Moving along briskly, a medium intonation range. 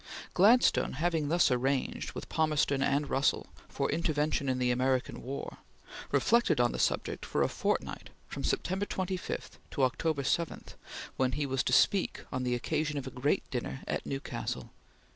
No: average, 160 wpm; average, 3.8 semitones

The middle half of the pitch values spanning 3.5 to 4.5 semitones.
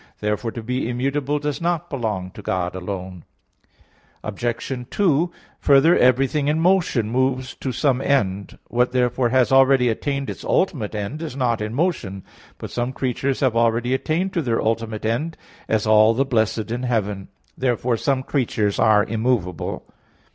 Yes: average, 3.9 semitones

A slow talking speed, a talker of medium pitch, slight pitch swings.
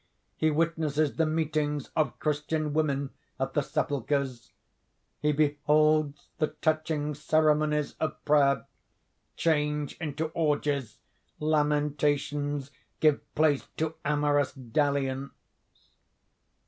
Yes: slow, 95 wpm; medium, 150 Hz; narrow, 1.4 semitones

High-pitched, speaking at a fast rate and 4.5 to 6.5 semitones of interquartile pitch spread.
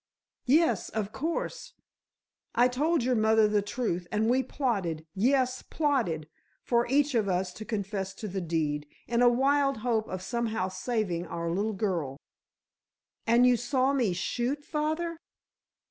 No: high, 225 Hz; average, 145 wpm; average, 5.3 semitones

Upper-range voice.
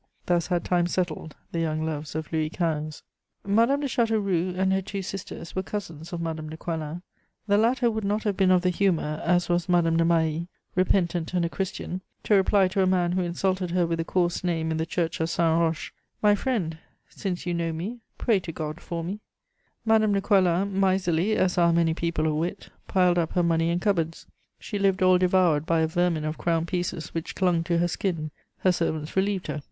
No: medium, 175 Hz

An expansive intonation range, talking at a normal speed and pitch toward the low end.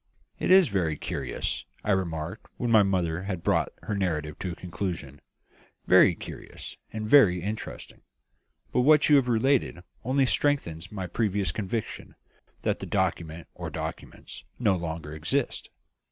Yes: wide, 5.7 semitones; average, 145 wpm; very low, 95 Hz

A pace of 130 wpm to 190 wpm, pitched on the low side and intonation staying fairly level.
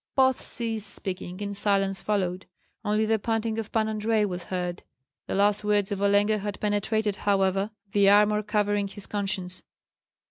No: average, 155 wpm; high, 205 Hz; narrow, 1.5 semitones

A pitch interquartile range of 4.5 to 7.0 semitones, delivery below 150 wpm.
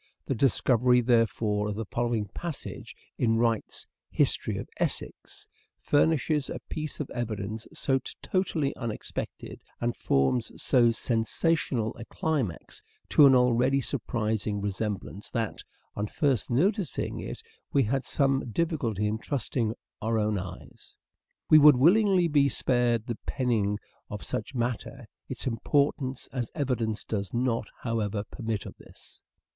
No: average, 4.1 semitones; average, 140 wpm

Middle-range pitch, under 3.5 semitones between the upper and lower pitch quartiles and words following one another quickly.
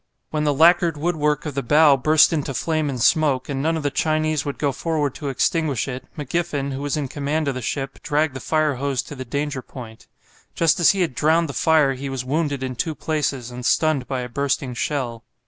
Yes: medium, 145 Hz; average, 2.8 semitones; fast, 225 wpm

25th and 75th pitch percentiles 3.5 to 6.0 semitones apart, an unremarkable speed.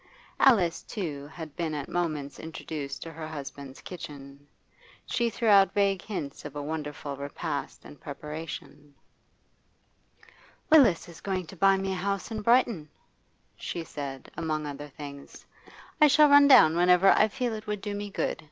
Yes: wide, 5.5 semitones; average, 160 wpm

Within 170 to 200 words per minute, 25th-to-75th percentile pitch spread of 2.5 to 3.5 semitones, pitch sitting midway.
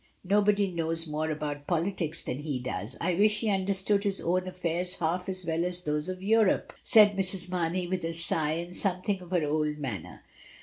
Yes: average, 190 wpm; average, 3.1 semitones; medium, 180 Hz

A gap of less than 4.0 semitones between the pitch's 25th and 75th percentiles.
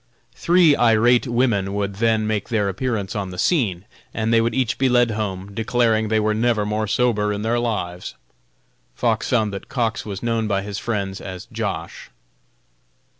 Yes: average, 2.9 semitones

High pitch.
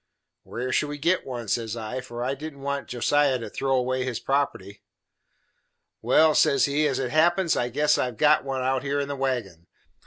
No: low, 135 Hz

